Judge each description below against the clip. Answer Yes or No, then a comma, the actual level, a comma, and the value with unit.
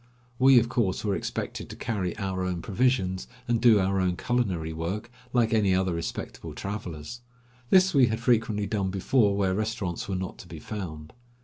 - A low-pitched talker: Yes, low, 100 Hz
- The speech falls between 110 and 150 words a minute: No, average, 180 wpm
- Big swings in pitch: No, average, 4.0 semitones